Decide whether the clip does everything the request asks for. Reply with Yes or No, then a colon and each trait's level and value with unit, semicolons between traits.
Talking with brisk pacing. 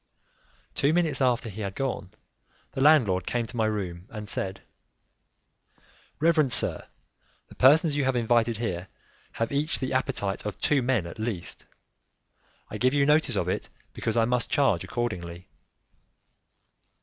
No: average, 150 wpm